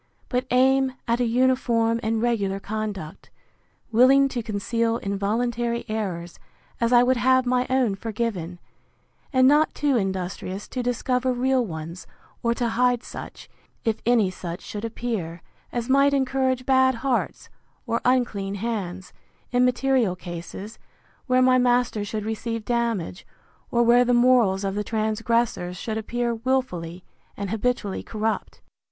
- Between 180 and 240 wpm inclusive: No, average, 140 wpm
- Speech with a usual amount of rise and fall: Yes, average, 3.6 semitones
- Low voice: No, high, 235 Hz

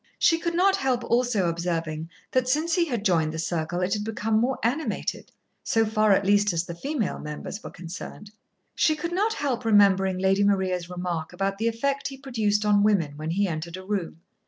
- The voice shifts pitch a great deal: Yes, wide, 5.7 semitones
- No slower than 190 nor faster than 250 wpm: Yes, average, 200 wpm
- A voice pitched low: No, high, 205 Hz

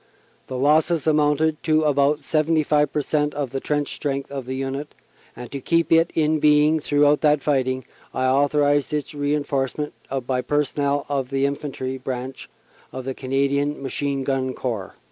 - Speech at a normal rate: Yes, average, 160 wpm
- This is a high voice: No, medium, 145 Hz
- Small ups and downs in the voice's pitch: Yes, narrow, 1.9 semitones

